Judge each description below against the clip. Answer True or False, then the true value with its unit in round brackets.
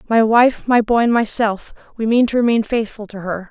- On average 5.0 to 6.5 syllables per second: True (5.2 syllables/s)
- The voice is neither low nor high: False (225 Hz)